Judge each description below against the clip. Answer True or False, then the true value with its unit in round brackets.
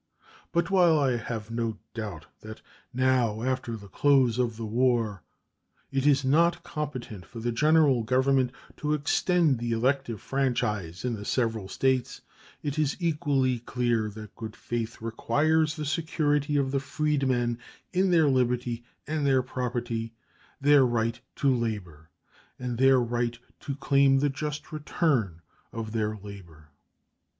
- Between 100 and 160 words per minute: True (140 wpm)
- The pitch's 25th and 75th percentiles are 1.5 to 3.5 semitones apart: False (4.0 semitones)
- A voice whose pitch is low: True (125 Hz)